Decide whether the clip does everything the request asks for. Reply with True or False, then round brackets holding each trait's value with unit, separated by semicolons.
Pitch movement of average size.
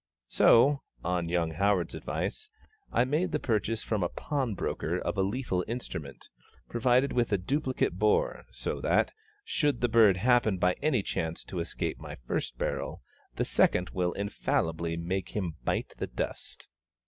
False (5.8 semitones)